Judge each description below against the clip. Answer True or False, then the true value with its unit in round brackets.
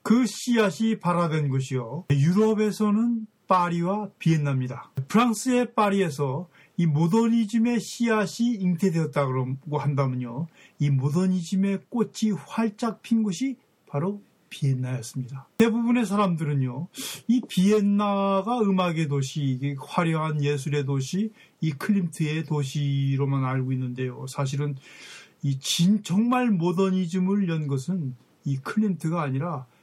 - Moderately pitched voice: True (175 Hz)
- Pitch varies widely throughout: True (6.9 semitones)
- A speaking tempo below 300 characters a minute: True (280 characters per minute)